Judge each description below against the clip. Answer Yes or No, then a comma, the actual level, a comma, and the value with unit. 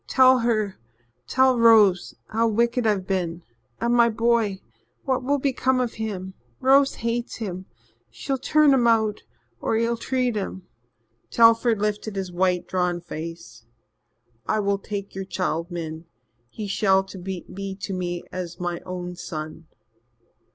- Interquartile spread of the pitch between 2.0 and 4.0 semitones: No, average, 4.6 semitones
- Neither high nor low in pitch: No, high, 200 Hz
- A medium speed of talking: Yes, average, 145 wpm